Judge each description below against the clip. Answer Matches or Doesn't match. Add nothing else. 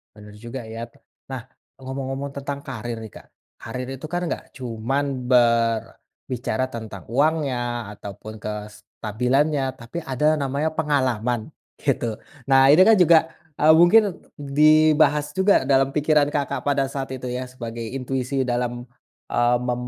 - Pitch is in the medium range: Doesn't match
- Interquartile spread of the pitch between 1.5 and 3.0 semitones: Doesn't match